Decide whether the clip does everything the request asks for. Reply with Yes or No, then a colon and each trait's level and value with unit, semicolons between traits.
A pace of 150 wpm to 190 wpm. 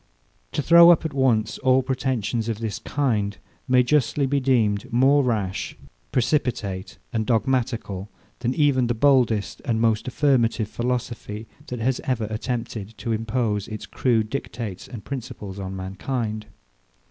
No: average, 140 wpm